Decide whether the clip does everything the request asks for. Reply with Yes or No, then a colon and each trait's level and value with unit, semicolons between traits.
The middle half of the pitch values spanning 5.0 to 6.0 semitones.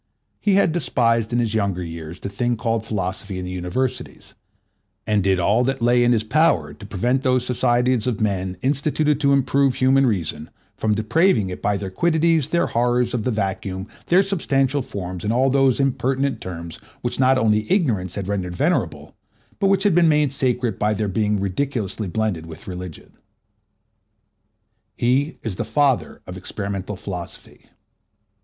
Yes: wide, 5.6 semitones